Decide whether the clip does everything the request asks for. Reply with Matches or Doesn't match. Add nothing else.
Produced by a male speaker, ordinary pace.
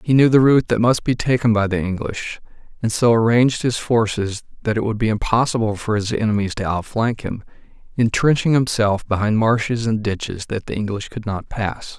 Matches